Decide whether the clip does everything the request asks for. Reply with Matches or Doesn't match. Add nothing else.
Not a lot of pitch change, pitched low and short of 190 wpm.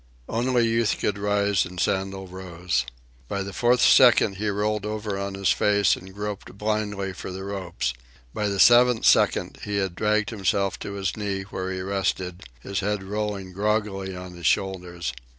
Matches